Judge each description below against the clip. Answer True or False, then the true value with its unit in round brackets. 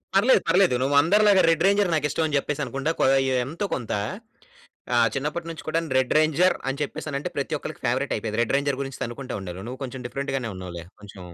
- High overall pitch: False (140 Hz)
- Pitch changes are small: False (4.8 semitones)